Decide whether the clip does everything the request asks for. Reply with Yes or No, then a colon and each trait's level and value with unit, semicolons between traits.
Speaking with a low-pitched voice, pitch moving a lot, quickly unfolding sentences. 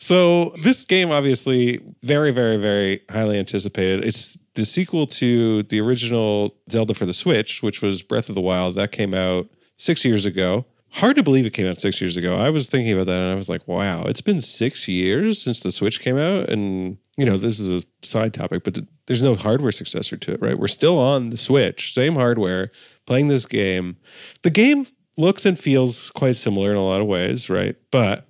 Yes: low, 115 Hz; wide, 5.8 semitones; fast, 210 wpm